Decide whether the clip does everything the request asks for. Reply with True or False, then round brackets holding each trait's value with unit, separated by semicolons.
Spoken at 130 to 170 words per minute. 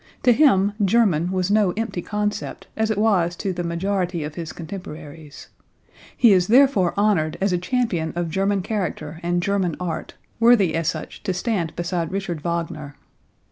True (165 wpm)